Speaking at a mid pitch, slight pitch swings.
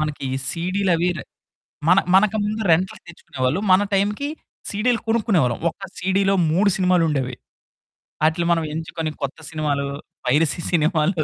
No: medium, 170 Hz; average, 4.1 semitones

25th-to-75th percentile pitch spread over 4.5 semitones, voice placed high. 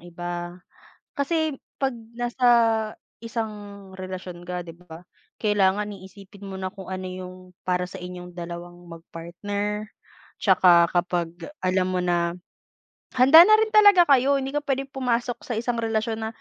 Yes: average, 5.2 semitones; high, 195 Hz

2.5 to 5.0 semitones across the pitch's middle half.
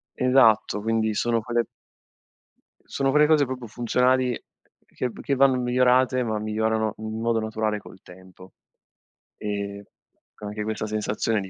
Yes: average, 2.9 semitones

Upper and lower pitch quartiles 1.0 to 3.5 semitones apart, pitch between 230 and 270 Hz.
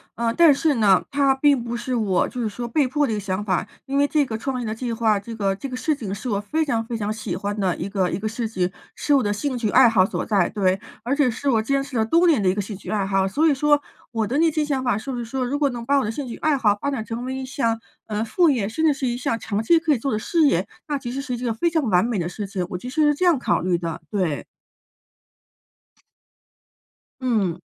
No: average, 5.2 semitones; high, 235 Hz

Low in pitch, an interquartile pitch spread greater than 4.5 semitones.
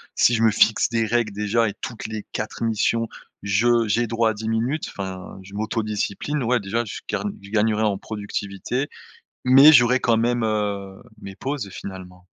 No: low, 110 Hz; average, 2.7 semitones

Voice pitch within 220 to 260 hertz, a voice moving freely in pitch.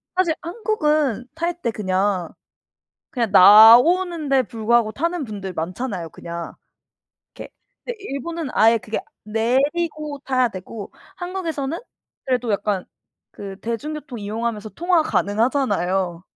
Yes: high, 240 Hz; wide, 7.0 semitones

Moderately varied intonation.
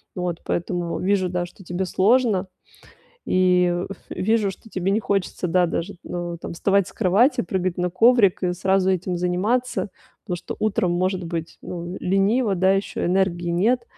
No: narrow, 2.0 semitones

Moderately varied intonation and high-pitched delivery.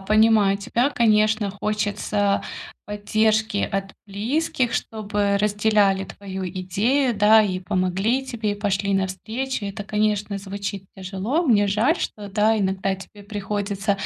No: narrow, 1.8 semitones; high, 205 Hz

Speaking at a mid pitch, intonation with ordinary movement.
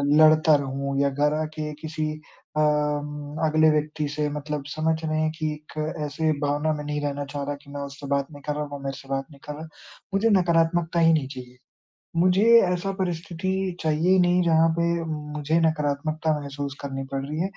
No: medium, 150 Hz; narrow, 2.1 semitones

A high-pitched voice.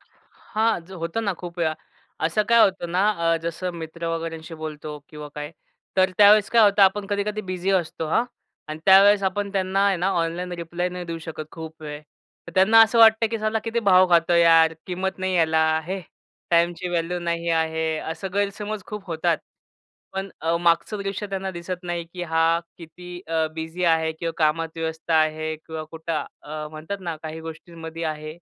No: medium, 170 Hz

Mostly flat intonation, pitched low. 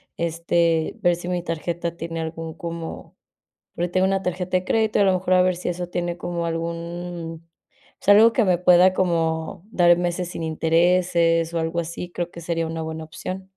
No: narrow, 1.5 semitones; medium, 170 Hz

